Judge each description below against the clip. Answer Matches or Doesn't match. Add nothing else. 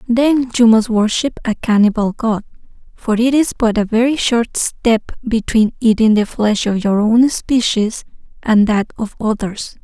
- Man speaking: Doesn't match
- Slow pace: Doesn't match